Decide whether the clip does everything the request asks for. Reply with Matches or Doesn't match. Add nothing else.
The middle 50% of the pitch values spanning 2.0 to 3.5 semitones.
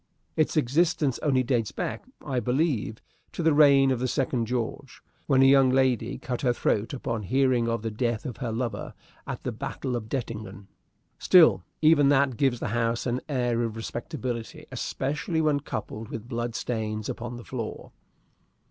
Matches